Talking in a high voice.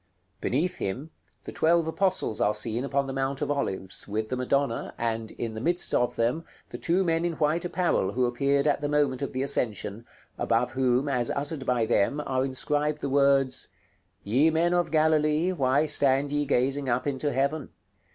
No: medium, 140 Hz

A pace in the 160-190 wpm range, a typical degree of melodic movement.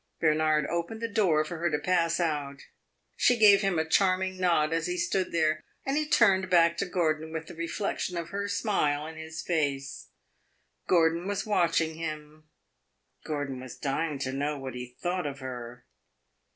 Yes: average, 175 wpm; average, 3.5 semitones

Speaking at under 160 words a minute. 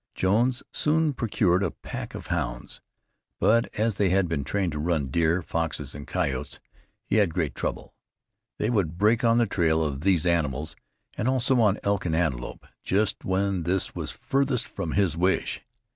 No: average, 175 wpm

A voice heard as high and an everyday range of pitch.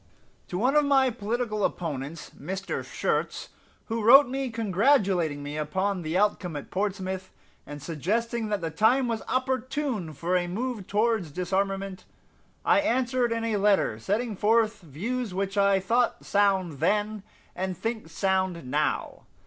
Yes: high, 200 Hz; average, 4.3 semitones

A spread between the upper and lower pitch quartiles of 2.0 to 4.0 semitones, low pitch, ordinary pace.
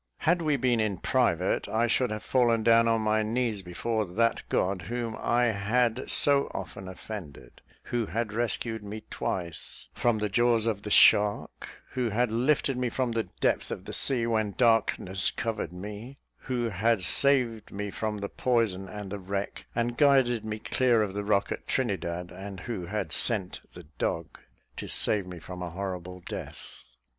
Yes: average, 3.2 semitones; low, 110 Hz; average, 175 wpm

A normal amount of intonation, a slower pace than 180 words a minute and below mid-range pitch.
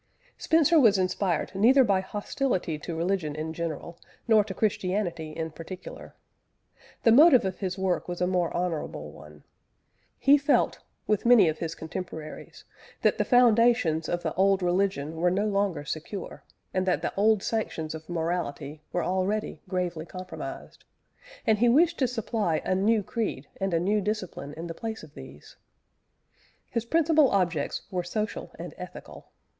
No: average, 4.7 semitones; average, 160 wpm; medium, 185 Hz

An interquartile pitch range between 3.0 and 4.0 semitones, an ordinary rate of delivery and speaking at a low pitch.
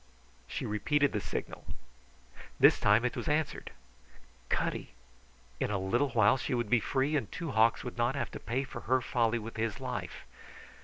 Yes: average, 3.4 semitones; average, 175 wpm; low, 120 Hz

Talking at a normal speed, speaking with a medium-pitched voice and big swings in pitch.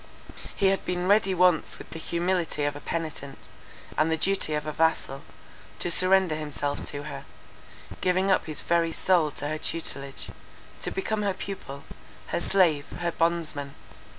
No: average, 160 wpm; medium, 165 Hz; average, 3.6 semitones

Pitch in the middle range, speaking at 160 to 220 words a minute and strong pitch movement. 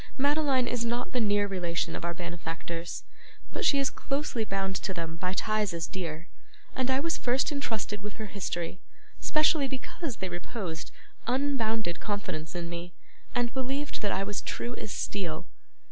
No: high, 205 Hz; average, 170 wpm; wide, 6.8 semitones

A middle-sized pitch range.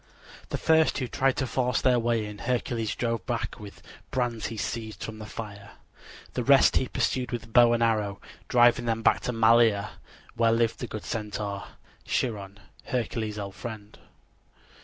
No: narrow, 2.2 semitones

